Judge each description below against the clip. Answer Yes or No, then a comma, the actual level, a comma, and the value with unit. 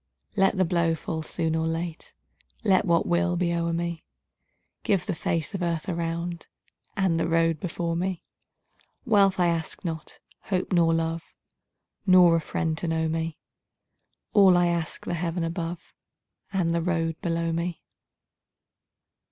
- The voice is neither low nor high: Yes, medium, 170 Hz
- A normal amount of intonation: No, narrow, 1.5 semitones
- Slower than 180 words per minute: Yes, average, 150 wpm